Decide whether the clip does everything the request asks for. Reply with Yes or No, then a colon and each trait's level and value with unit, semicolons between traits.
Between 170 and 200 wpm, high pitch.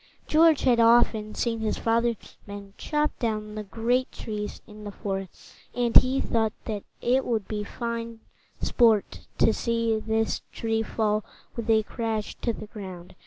No: average, 160 wpm; high, 225 Hz